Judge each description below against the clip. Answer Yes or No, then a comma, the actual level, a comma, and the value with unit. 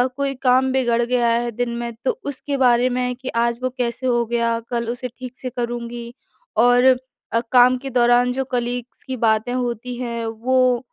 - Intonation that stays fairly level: Yes, narrow, 1.2 semitones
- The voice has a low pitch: No, high, 245 Hz